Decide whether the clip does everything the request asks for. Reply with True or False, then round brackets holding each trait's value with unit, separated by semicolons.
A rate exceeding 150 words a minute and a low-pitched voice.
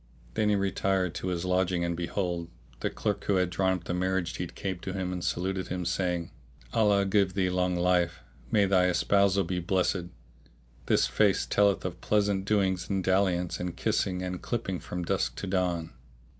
True (185 wpm; 90 Hz)